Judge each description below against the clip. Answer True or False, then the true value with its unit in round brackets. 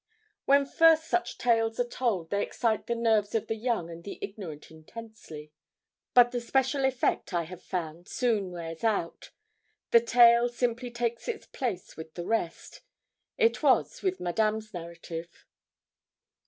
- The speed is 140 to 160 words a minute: True (150 wpm)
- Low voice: False (225 Hz)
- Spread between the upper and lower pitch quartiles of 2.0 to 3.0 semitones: False (5.6 semitones)